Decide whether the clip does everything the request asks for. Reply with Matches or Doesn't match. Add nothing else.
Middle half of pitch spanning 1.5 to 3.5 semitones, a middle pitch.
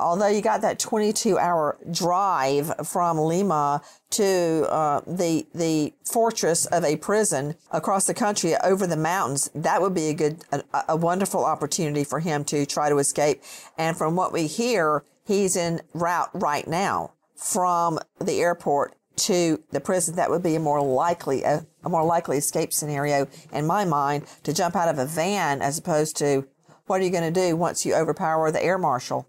Matches